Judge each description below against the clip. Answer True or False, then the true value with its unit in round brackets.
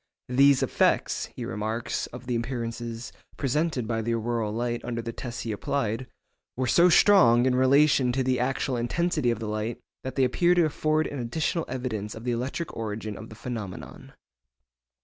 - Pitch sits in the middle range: False (120 Hz)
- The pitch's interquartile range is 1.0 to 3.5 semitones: True (2.9 semitones)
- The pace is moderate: True (175 wpm)